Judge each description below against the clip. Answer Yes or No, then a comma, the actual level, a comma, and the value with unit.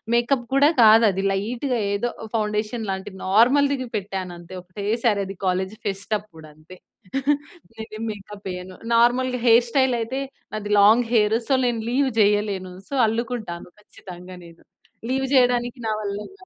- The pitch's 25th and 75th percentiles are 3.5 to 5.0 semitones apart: Yes, average, 3.9 semitones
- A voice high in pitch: Yes, high, 215 Hz